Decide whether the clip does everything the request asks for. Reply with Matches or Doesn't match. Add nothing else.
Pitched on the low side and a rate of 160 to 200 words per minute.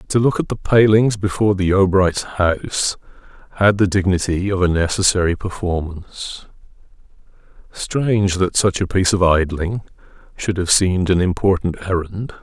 Doesn't match